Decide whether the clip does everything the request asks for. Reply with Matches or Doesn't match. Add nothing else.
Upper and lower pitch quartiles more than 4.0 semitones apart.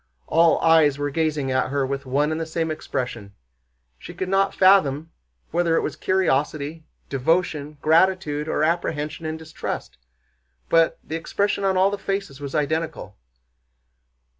Doesn't match